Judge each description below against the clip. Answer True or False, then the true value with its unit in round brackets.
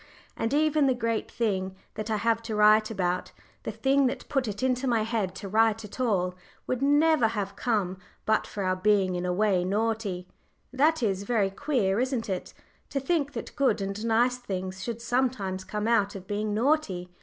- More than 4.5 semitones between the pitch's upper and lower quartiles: False (4.2 semitones)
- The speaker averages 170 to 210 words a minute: True (190 wpm)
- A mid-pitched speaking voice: False (220 Hz)